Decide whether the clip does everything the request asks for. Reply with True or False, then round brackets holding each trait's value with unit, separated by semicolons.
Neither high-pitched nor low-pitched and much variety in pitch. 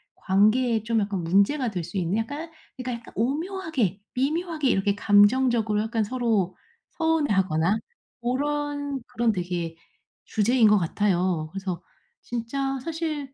False (225 Hz; 5.8 semitones)